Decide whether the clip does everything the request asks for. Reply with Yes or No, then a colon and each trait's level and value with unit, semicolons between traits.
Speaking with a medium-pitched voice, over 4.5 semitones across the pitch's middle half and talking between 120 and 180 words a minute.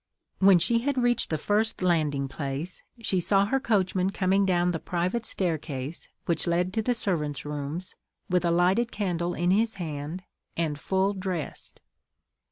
No: medium, 180 Hz; average, 3.6 semitones; average, 160 wpm